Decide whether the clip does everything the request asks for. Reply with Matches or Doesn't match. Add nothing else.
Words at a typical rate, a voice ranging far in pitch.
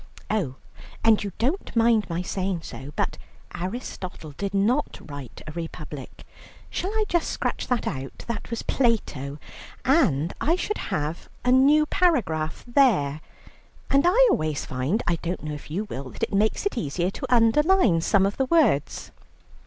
Matches